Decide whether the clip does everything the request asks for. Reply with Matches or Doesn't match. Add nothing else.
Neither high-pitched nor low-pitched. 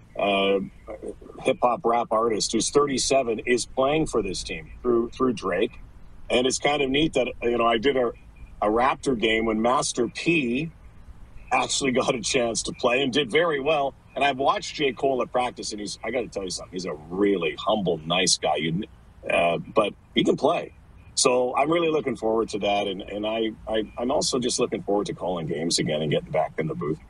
Doesn't match